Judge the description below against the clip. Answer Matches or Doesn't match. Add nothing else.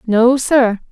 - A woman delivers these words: Matches